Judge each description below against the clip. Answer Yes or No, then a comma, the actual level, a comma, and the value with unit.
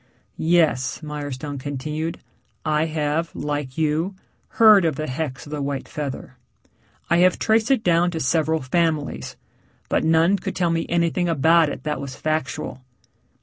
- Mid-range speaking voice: Yes, medium, 155 Hz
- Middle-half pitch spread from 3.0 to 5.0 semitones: No, narrow, 2.6 semitones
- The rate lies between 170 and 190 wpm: No, average, 150 wpm